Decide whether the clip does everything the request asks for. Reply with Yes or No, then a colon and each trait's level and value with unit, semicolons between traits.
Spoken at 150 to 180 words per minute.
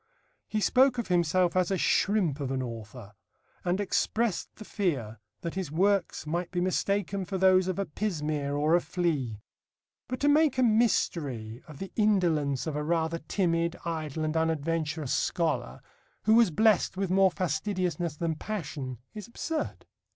Yes: average, 160 wpm